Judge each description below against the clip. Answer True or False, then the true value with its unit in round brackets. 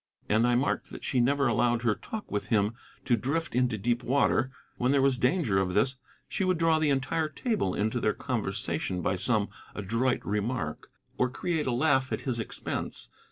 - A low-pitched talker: True (125 Hz)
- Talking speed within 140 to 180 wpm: False (190 wpm)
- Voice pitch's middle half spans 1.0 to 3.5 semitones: False (4.2 semitones)